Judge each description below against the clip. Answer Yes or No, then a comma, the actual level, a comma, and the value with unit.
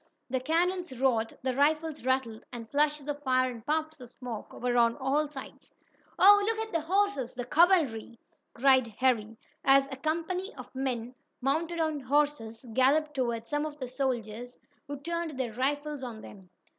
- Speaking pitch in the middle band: No, very high, 270 Hz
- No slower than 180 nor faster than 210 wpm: No, average, 170 wpm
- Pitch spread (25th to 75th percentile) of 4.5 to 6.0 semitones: No, average, 3.9 semitones